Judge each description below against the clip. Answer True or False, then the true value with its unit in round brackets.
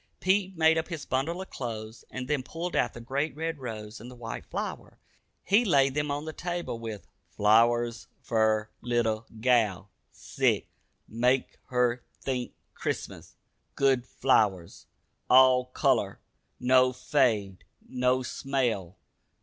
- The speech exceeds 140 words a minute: False (135 wpm)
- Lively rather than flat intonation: False (3.9 semitones)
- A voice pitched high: False (125 Hz)